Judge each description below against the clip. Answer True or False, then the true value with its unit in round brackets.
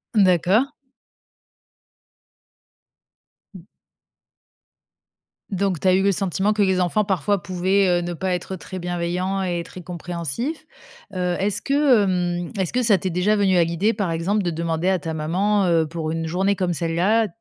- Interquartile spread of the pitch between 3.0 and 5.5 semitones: False (2.6 semitones)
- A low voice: False (185 Hz)